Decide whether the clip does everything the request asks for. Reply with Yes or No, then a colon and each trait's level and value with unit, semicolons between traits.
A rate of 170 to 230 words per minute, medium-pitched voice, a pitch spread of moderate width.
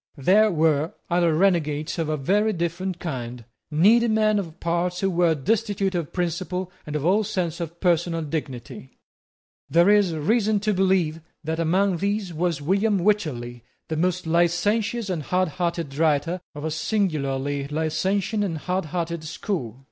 No: average, 150 wpm; medium, 170 Hz; average, 3.8 semitones